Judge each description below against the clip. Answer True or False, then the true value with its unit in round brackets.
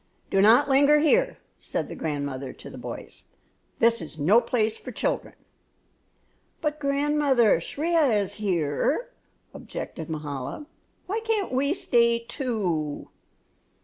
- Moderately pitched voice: False (235 Hz)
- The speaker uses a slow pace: True (120 wpm)